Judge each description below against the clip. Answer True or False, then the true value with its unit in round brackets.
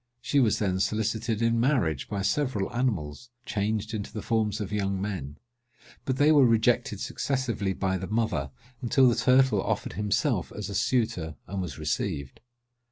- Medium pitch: False (105 Hz)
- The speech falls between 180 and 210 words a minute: False (165 wpm)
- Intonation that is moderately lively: True (3.8 semitones)